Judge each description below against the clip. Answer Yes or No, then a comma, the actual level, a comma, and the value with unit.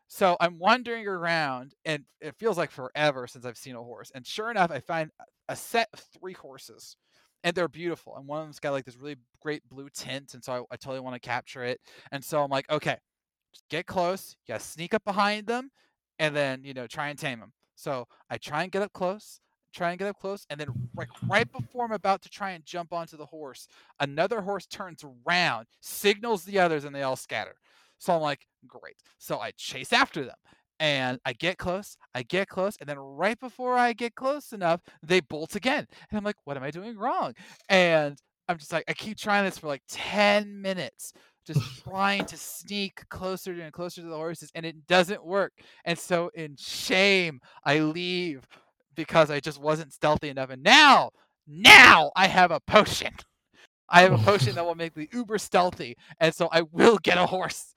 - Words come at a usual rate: No, fast, 210 wpm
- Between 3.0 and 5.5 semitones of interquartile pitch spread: Yes, average, 5.0 semitones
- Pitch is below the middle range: No, medium, 165 Hz